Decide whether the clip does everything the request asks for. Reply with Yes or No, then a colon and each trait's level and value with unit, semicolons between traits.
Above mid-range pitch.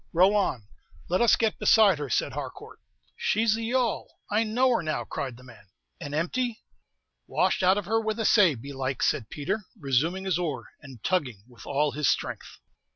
No: medium, 175 Hz